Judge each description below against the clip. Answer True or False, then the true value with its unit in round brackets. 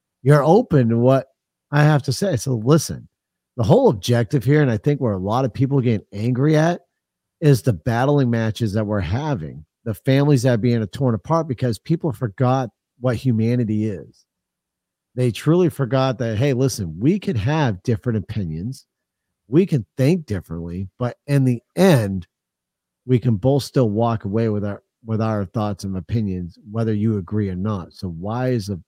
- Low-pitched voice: True (120 Hz)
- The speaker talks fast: False (180 wpm)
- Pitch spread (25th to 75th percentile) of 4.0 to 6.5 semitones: True (4.6 semitones)